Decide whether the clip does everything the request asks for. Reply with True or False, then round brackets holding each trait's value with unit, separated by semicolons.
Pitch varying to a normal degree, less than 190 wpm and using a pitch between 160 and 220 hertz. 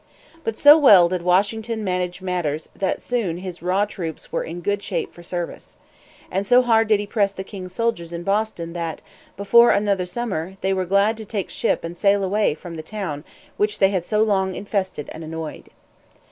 False (3.2 semitones; 195 wpm; 190 Hz)